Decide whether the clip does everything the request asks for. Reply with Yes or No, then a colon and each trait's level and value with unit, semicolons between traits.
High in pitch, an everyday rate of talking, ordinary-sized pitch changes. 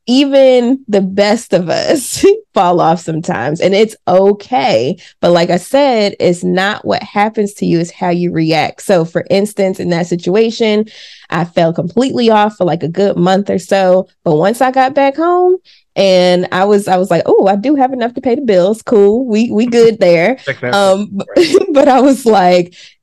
Yes: high, 200 Hz; average, 190 wpm; average, 4.9 semitones